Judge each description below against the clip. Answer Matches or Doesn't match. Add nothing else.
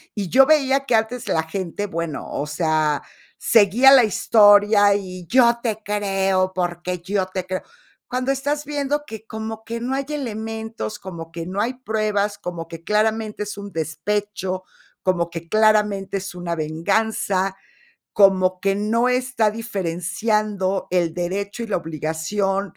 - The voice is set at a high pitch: Matches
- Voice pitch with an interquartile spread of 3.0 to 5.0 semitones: Matches